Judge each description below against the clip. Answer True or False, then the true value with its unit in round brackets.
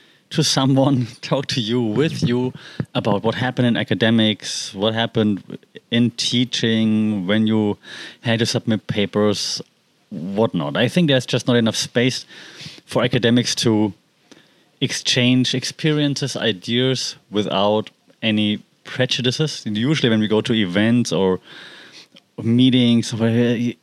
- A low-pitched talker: True (120 Hz)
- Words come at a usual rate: False (120 wpm)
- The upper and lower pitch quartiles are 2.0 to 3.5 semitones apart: True (2.9 semitones)